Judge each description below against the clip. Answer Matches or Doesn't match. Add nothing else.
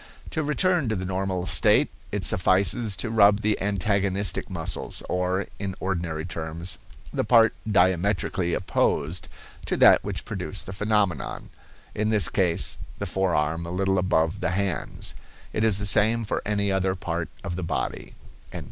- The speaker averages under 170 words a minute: Matches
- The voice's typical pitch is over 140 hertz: Doesn't match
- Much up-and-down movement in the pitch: Doesn't match